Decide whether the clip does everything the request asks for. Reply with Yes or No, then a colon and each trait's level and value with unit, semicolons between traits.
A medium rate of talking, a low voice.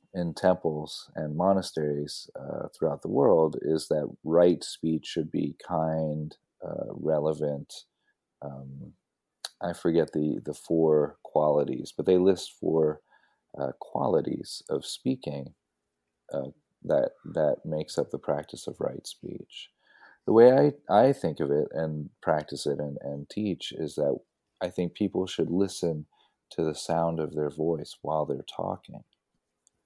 Yes: average, 145 wpm; very low, 80 Hz